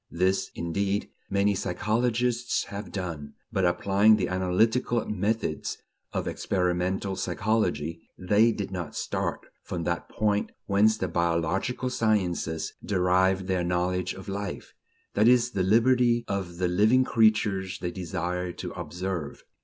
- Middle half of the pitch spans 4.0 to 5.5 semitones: No, average, 3.3 semitones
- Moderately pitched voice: No, very low, 95 Hz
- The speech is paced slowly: Yes, slow, 130 wpm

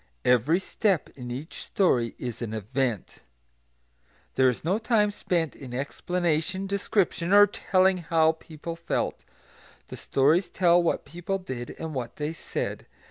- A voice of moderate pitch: Yes, medium, 165 Hz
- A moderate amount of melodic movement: No, wide, 6.0 semitones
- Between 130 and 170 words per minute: Yes, average, 140 wpm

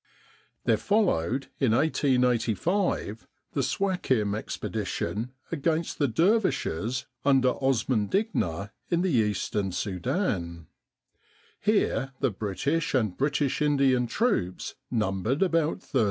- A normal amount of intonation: No, wide, 7.3 semitones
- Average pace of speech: No, slow, 100 wpm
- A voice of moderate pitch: No, low, 130 Hz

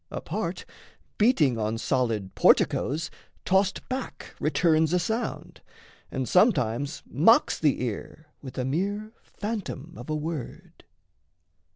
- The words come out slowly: Yes, slow, 115 wpm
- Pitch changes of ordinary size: No, wide, 6.9 semitones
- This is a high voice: No, medium, 155 Hz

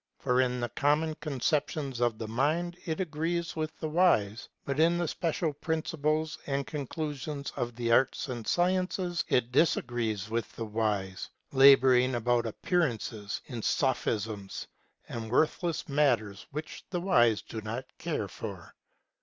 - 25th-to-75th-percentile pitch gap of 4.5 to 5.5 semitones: Yes, average, 5.2 semitones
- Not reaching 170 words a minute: Yes, average, 140 wpm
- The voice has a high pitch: No, low, 135 Hz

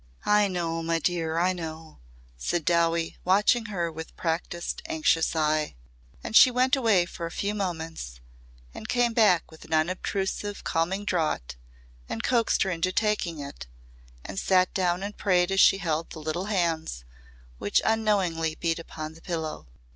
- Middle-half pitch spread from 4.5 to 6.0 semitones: No, average, 3.5 semitones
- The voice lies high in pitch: No, medium, 175 Hz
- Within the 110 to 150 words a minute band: No, average, 160 wpm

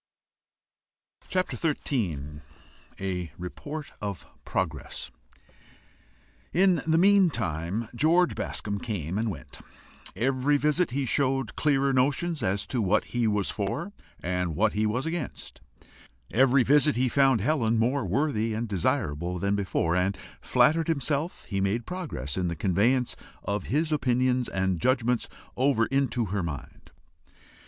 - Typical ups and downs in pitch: No, wide, 6.4 semitones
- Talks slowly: Yes, slow, 130 wpm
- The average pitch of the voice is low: Yes, low, 120 Hz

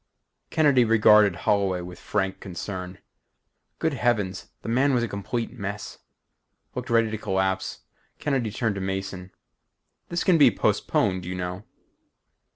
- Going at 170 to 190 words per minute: No, slow, 135 wpm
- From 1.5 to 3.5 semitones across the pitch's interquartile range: No, average, 4.1 semitones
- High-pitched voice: No, low, 100 Hz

